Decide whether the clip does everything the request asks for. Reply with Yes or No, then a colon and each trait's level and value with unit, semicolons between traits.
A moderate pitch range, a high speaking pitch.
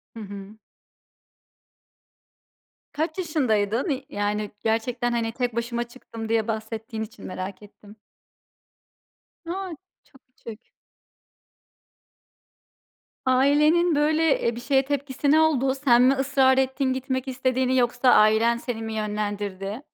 Yes: average, 3.6 semitones; high, 245 Hz